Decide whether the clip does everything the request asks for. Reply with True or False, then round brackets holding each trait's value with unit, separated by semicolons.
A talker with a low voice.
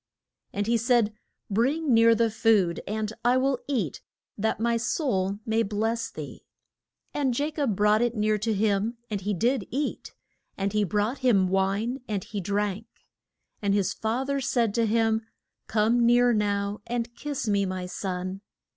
False (220 Hz)